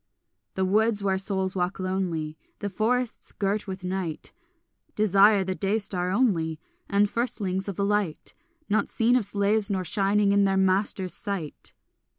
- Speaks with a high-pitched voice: Yes, high, 195 Hz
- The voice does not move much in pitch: Yes, narrow, 1.8 semitones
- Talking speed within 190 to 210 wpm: No, average, 155 wpm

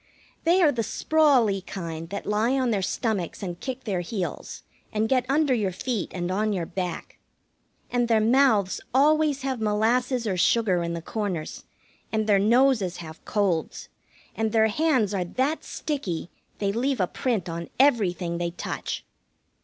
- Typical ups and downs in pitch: No, wide, 5.8 semitones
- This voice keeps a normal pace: Yes, average, 160 wpm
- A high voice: Yes, high, 215 Hz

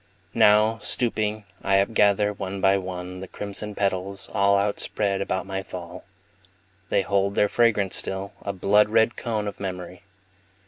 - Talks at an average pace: Yes, average, 145 wpm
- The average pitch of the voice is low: Yes, low, 100 Hz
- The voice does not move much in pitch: Yes, narrow, 1.4 semitones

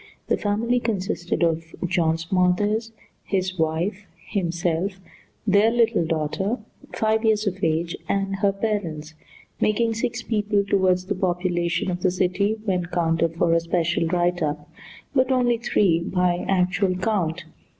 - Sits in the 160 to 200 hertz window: Yes, medium, 185 Hz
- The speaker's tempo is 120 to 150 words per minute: Yes, average, 140 wpm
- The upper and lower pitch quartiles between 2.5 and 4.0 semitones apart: Yes, average, 3.4 semitones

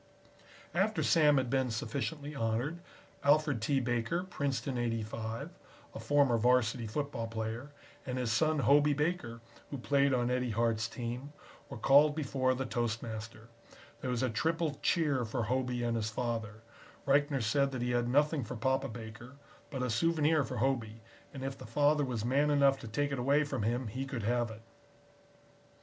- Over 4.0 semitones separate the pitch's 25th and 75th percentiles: No, average, 3.6 semitones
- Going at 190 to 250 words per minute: No, average, 170 wpm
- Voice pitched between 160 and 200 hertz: No, low, 130 Hz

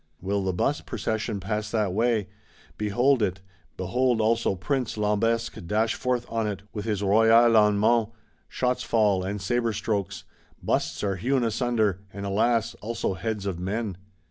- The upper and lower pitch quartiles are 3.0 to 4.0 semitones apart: No, narrow, 2.6 semitones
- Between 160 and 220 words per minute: No, average, 150 wpm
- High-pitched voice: No, low, 110 Hz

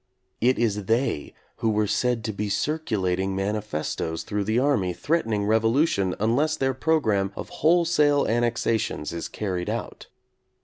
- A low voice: Yes, low, 110 Hz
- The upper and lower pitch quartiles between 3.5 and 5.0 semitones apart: No, wide, 5.4 semitones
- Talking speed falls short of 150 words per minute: Yes, average, 140 wpm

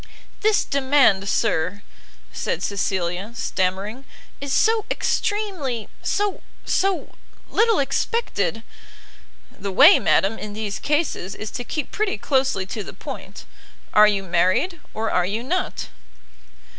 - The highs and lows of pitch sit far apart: Yes, wide, 7.8 semitones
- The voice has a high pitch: Yes, high, 225 Hz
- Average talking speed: No, slow, 125 wpm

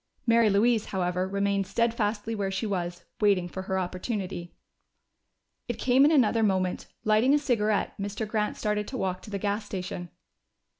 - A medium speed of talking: Yes, average, 160 wpm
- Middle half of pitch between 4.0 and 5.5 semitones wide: No, average, 2.9 semitones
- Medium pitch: No, high, 205 Hz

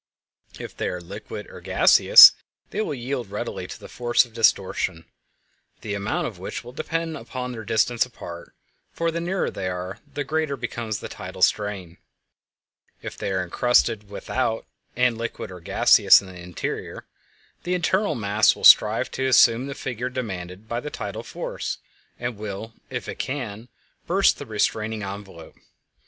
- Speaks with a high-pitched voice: No, low, 115 Hz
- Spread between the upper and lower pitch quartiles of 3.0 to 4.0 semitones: No, average, 4.4 semitones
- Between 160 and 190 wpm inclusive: Yes, average, 165 wpm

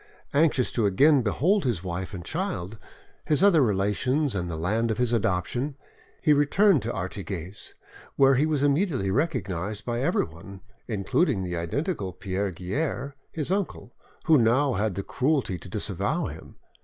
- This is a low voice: Yes, low, 115 Hz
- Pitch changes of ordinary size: No, wide, 7.2 semitones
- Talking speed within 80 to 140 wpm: No, average, 155 wpm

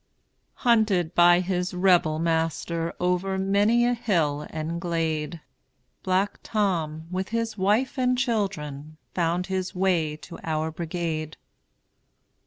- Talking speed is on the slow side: Yes, slow, 115 wpm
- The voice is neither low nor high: Yes, medium, 180 Hz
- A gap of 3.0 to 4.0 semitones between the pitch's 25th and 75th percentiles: Yes, average, 3.4 semitones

